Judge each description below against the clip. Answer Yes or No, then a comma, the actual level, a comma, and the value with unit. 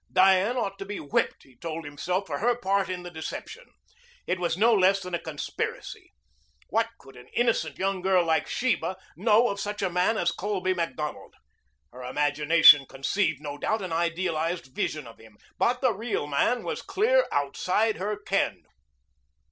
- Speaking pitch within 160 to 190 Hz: Yes, medium, 185 Hz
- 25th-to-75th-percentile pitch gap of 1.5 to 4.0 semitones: No, average, 4.9 semitones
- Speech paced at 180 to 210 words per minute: No, average, 170 wpm